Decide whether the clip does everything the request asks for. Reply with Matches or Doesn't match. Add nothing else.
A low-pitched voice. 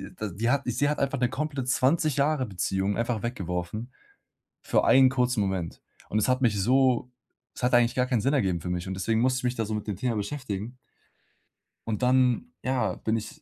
Matches